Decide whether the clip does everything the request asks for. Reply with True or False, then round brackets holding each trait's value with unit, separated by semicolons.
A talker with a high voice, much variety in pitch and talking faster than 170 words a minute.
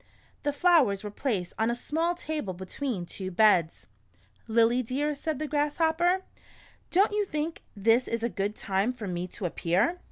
False (240 Hz; 7.5 semitones; 165 wpm)